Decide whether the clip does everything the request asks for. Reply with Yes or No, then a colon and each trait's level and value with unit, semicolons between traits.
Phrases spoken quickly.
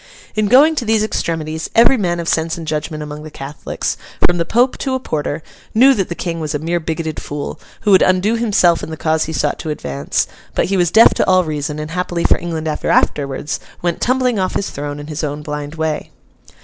Yes: fast, 225 wpm